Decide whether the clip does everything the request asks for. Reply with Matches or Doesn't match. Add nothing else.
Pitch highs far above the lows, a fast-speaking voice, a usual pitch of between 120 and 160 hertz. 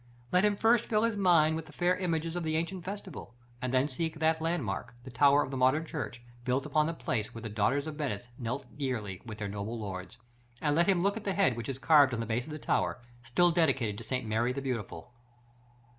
Matches